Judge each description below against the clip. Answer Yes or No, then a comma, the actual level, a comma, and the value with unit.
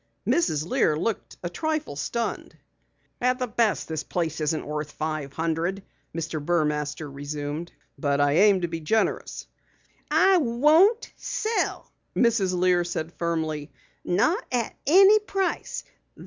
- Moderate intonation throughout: No, wide, 7.7 semitones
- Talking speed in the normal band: No, slow, 125 wpm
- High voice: No, medium, 175 Hz